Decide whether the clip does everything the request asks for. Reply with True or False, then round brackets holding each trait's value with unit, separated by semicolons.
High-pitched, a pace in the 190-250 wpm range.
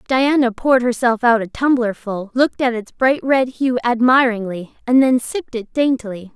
False (240 Hz; 170 wpm)